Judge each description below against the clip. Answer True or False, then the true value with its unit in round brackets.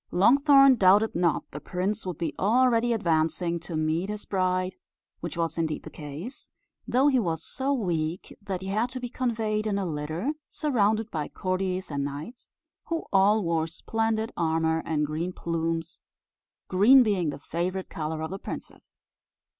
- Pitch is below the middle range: False (185 Hz)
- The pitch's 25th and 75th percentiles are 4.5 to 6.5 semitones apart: True (5.3 semitones)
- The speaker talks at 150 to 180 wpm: True (160 wpm)